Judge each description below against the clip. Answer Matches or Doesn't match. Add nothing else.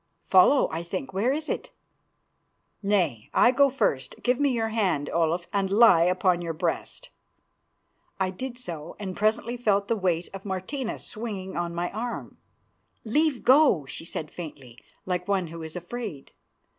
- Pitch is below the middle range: Doesn't match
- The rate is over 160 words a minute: Doesn't match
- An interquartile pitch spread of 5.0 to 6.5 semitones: Matches